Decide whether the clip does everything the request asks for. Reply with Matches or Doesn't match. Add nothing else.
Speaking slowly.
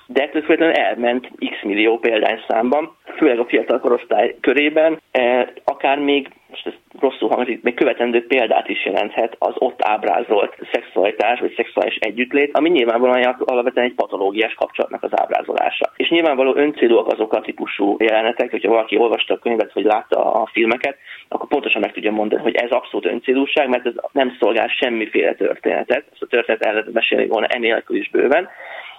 Doesn't match